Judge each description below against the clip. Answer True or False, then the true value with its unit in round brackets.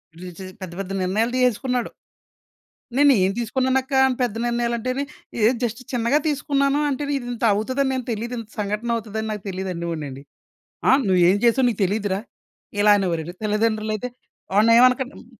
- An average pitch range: True (4.0 semitones)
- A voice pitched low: False (230 Hz)